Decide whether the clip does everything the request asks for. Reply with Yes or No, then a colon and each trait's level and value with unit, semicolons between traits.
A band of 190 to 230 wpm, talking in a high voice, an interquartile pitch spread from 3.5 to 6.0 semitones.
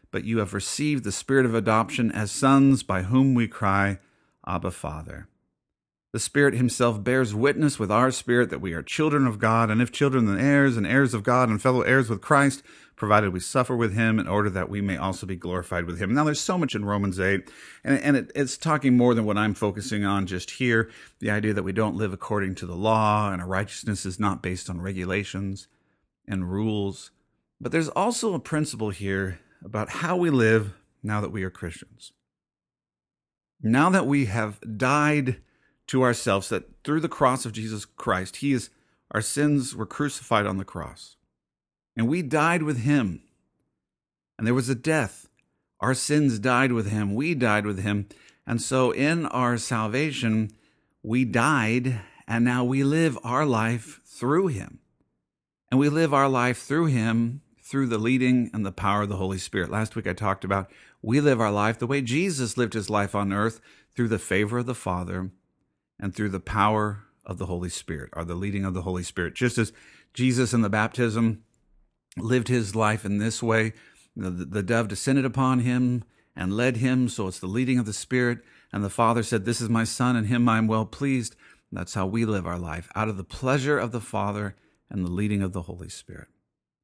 No: average, 200 wpm; low, 110 Hz; average, 4.4 semitones